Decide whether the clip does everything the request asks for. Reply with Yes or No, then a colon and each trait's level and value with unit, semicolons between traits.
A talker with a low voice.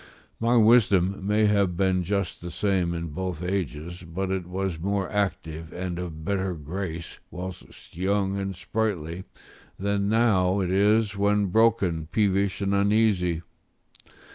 Yes: very low, 95 Hz